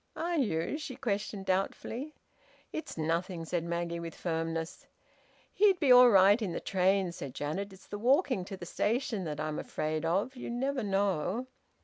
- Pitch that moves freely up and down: Yes, wide, 6.5 semitones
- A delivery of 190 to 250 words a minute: No, average, 165 wpm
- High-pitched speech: Yes, high, 195 Hz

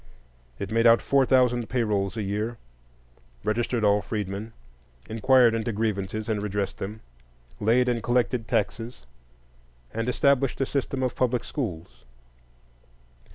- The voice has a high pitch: No, low, 115 Hz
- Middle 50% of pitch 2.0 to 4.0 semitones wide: Yes, average, 3.0 semitones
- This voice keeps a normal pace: No, slow, 130 wpm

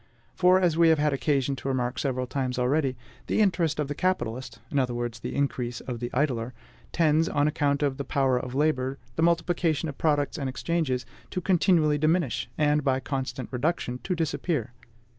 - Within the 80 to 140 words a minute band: No, average, 185 wpm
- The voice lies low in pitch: No, medium, 145 Hz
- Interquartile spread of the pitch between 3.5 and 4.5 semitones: Yes, average, 3.9 semitones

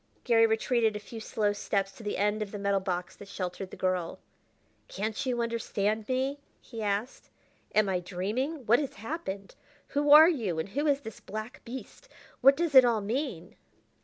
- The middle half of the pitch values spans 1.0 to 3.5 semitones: No, average, 4.4 semitones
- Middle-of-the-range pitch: No, high, 220 Hz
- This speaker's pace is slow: No, average, 185 wpm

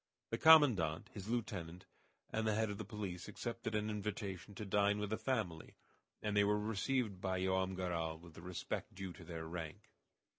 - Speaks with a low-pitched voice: Yes, low, 100 Hz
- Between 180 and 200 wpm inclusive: Yes, average, 185 wpm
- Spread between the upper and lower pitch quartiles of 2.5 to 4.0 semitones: Yes, average, 3.2 semitones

